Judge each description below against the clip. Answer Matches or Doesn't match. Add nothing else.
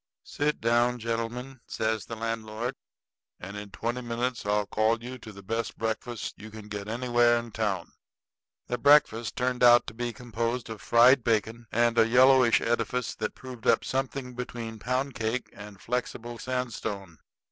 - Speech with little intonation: Matches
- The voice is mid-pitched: Doesn't match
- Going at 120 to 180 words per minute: Matches